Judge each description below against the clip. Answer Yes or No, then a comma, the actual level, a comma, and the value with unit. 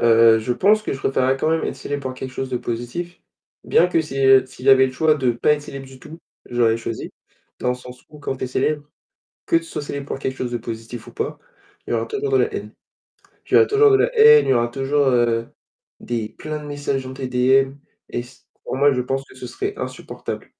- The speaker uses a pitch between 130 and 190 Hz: Yes, low, 135 Hz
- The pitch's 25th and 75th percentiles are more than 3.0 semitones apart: Yes, average, 3.5 semitones